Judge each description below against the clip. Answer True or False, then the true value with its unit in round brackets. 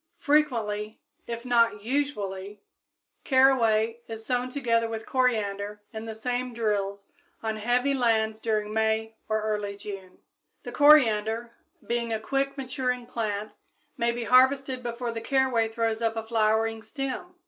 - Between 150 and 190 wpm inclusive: False (140 wpm)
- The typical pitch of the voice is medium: False (230 Hz)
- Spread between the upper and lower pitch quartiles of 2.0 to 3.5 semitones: True (2.6 semitones)